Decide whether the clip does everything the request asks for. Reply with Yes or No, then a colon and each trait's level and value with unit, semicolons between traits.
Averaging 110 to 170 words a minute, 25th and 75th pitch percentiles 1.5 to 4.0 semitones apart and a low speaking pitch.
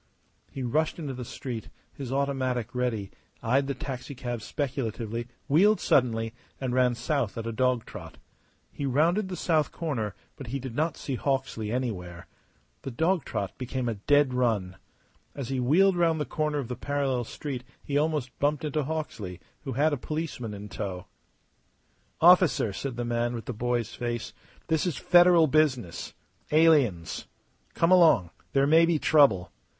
No: average, 160 wpm; average, 4.5 semitones; low, 130 Hz